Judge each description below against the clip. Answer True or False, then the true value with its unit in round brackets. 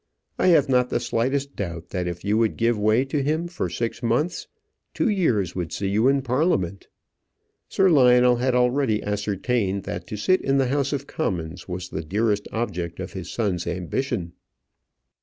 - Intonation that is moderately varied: False (6.4 semitones)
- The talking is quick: False (175 wpm)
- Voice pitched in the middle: False (115 Hz)